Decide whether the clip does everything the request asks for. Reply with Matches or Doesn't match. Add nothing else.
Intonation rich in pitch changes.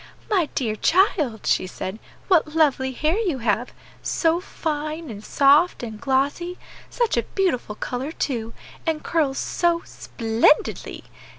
Matches